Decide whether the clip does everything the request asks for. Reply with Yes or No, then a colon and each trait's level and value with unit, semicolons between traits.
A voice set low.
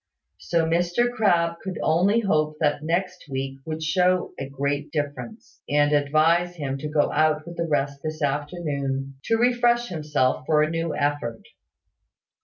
No: medium, 155 Hz